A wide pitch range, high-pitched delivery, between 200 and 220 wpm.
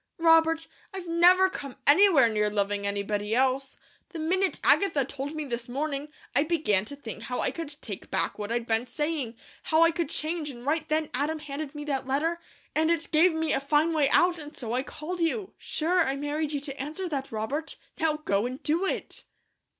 No: average, 4.1 semitones; very high, 295 Hz; fast, 205 wpm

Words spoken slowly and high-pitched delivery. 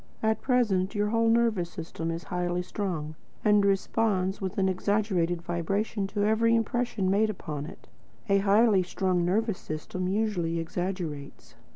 No: average, 145 wpm; high, 195 Hz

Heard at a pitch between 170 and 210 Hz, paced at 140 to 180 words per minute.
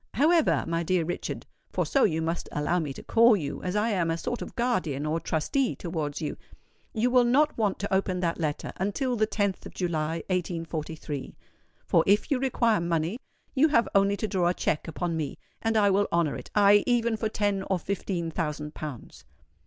No: medium, 185 Hz; average, 190 wpm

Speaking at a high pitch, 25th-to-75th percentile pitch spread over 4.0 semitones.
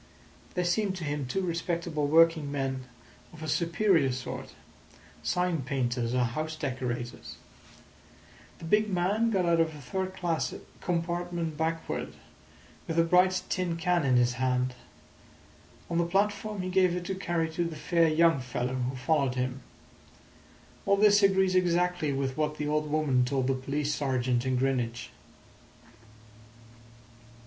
No: medium, 160 Hz; average, 5.1 semitones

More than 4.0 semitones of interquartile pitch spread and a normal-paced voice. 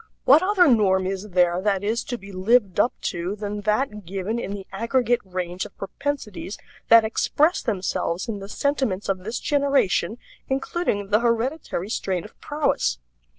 Yes: average, 4.6 semitones; average, 160 wpm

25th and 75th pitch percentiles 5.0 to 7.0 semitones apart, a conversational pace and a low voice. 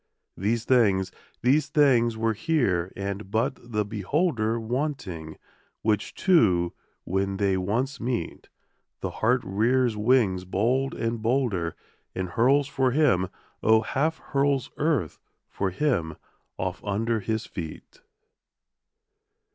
No: average, 5.3 semitones; slow, 115 wpm; low, 115 Hz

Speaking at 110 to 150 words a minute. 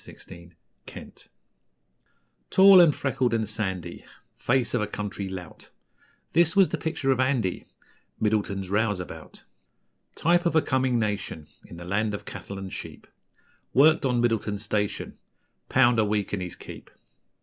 Yes: average, 145 wpm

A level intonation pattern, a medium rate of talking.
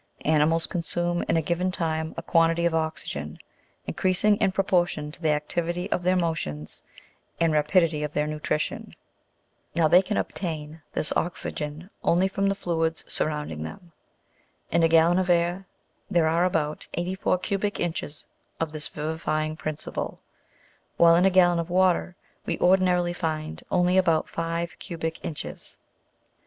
Yes: narrow, 2.3 semitones; average, 150 wpm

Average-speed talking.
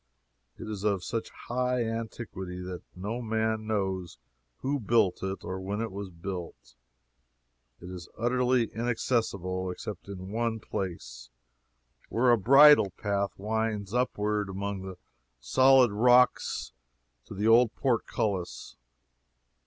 No: slow, 120 wpm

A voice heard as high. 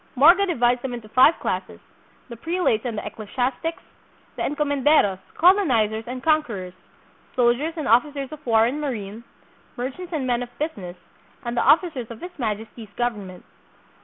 Yes: high, 245 Hz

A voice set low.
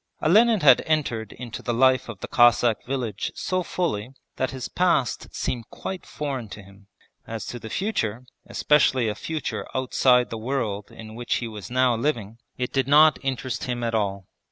Yes: low, 125 Hz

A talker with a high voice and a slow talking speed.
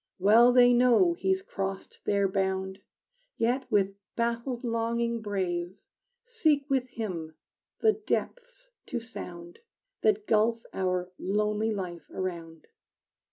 Yes: high, 220 Hz; slow, 115 wpm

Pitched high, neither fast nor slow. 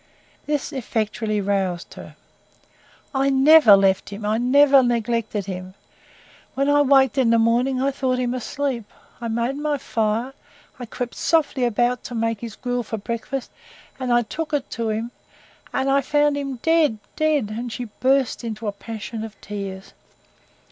Yes: high, 240 Hz; average, 155 wpm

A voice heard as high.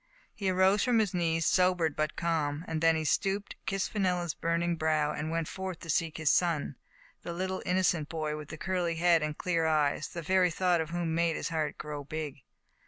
No: medium, 165 Hz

